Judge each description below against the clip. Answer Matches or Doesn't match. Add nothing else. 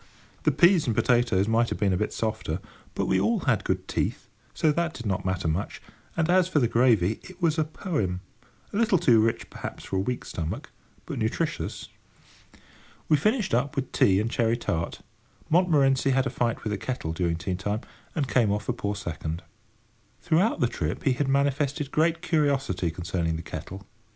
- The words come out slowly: Doesn't match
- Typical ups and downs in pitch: Doesn't match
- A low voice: Matches